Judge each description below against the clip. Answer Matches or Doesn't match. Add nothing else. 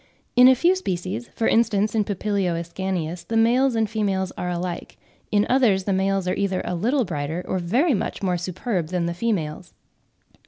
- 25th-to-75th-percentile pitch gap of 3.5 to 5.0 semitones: Matches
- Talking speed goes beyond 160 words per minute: Matches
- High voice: Matches